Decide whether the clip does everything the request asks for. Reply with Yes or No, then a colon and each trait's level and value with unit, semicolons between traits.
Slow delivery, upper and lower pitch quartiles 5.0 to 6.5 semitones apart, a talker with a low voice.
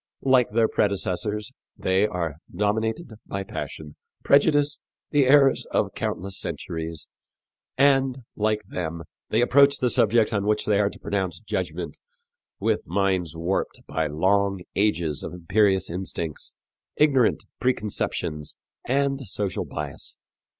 Yes: slow, 120 wpm; wide, 5.4 semitones; low, 105 Hz